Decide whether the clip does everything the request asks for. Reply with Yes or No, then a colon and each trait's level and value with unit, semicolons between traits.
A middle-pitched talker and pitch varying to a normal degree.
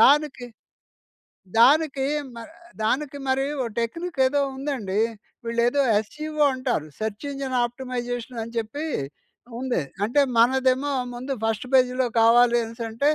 No: very high, 255 Hz; average, 3.1 semitones